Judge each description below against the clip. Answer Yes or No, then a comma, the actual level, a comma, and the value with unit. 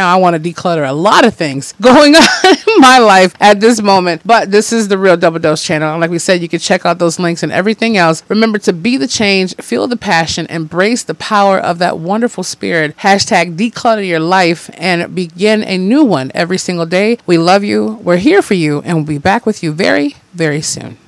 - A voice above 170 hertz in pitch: Yes, medium, 185 Hz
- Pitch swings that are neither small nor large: Yes, average, 4.6 semitones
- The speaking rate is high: Yes, fast, 230 wpm